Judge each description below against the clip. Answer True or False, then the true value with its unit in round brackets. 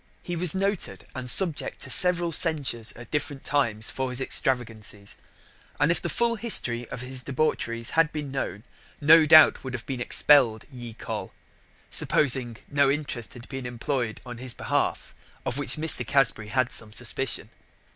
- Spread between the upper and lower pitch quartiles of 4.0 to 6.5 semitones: True (4.3 semitones)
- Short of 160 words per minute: False (165 wpm)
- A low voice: True (130 Hz)